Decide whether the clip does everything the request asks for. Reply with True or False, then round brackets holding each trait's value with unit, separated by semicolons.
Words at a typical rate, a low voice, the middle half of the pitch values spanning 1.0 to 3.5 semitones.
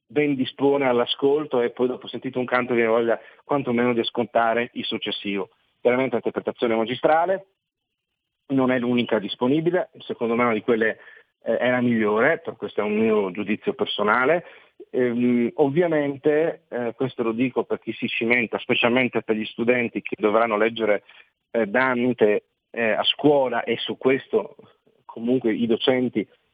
True (150 wpm; 120 Hz; 2.4 semitones)